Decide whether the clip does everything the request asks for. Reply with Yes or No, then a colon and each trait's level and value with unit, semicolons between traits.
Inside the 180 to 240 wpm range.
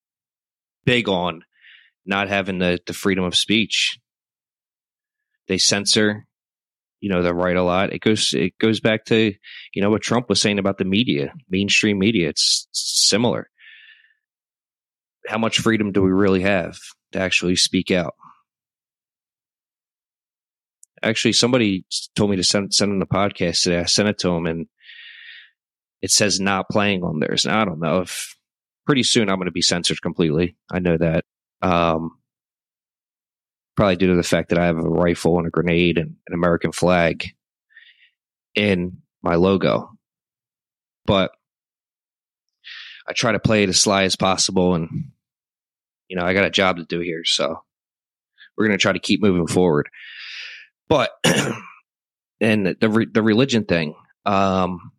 No: average, 155 wpm